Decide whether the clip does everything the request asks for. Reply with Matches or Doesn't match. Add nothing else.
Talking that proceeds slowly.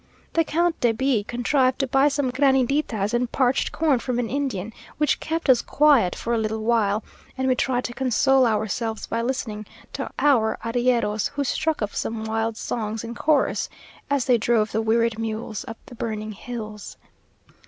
Doesn't match